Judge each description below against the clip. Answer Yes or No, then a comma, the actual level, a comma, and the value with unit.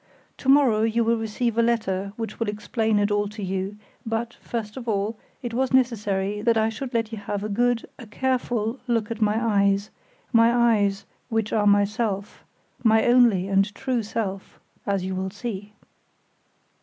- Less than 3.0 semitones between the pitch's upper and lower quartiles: Yes, narrow, 2.5 semitones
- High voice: Yes, high, 220 Hz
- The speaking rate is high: No, average, 175 wpm